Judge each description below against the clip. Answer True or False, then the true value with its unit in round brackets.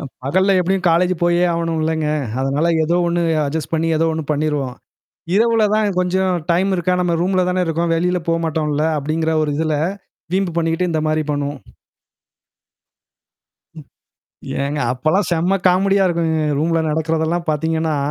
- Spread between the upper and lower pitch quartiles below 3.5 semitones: True (2.5 semitones)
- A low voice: False (165 Hz)